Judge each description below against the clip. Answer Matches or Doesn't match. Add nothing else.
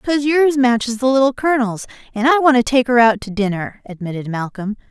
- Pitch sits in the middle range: Doesn't match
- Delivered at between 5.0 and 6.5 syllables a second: Matches